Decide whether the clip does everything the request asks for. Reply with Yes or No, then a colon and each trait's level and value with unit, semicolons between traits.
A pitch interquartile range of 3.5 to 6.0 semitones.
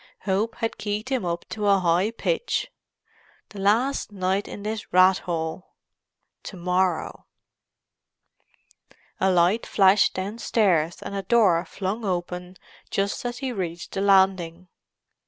No: average, 2.7 semitones